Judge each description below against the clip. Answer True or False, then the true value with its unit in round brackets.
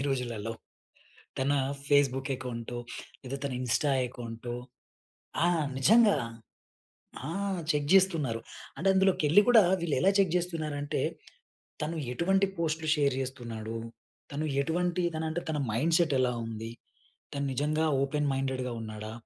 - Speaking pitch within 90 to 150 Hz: True (140 Hz)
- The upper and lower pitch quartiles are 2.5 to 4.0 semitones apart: False (4.9 semitones)